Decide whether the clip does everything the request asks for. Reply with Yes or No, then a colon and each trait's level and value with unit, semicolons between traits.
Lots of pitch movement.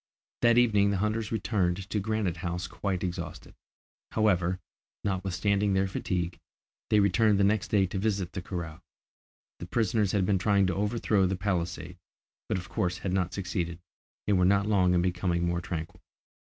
No: narrow, 2.6 semitones